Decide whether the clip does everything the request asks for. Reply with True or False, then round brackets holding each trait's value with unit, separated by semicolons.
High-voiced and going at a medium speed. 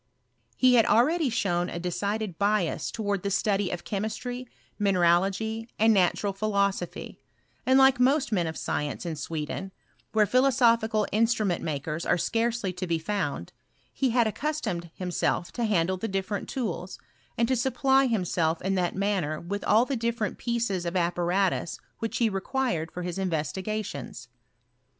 True (200 Hz; 150 wpm)